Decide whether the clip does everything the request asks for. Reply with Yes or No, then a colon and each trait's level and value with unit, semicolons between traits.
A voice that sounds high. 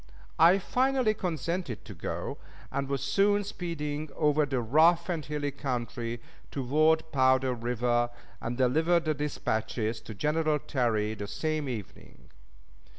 No: medium, 145 Hz